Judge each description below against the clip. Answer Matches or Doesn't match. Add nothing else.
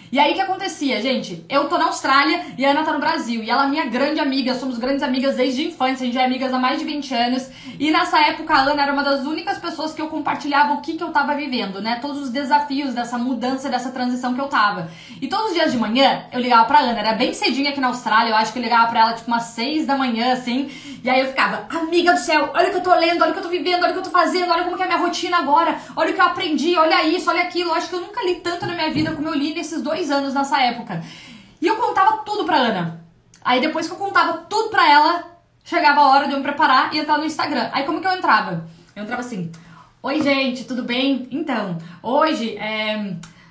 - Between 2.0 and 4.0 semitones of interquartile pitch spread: Doesn't match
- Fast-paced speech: Matches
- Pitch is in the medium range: Doesn't match